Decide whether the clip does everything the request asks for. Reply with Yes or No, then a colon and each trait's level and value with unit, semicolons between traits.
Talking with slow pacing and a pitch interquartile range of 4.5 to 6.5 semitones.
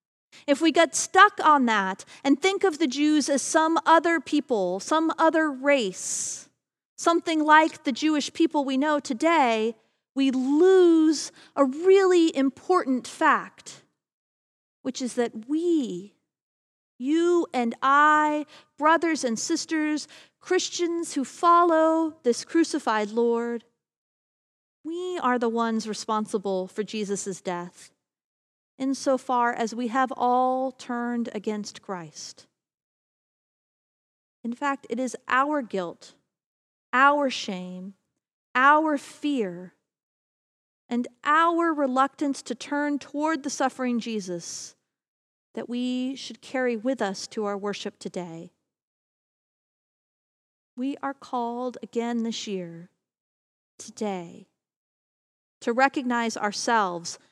Yes: slow, 110 wpm; wide, 5.5 semitones